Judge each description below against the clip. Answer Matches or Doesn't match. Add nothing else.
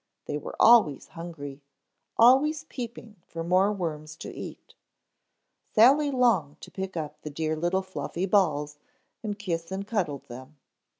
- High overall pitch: Doesn't match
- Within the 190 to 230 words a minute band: Doesn't match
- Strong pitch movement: Matches